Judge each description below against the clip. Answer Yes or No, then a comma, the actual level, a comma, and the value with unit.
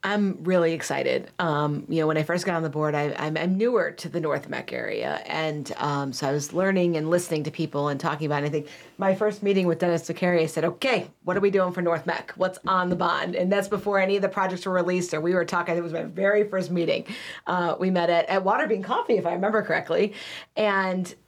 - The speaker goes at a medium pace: No, fast, 245 wpm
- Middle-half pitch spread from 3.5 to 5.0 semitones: No, average, 2.9 semitones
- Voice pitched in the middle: Yes, medium, 175 Hz